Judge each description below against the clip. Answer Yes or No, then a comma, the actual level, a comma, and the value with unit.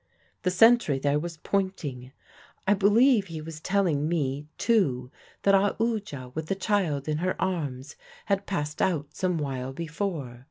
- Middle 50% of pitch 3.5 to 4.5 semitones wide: No, wide, 5.5 semitones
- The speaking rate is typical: Yes, average, 150 wpm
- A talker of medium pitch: Yes, medium, 165 Hz